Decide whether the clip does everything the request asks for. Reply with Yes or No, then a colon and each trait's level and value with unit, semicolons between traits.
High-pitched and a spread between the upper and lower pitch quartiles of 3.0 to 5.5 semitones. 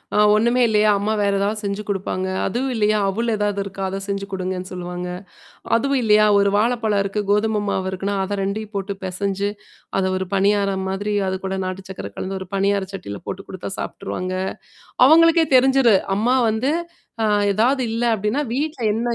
No: high, 205 Hz; narrow, 2.5 semitones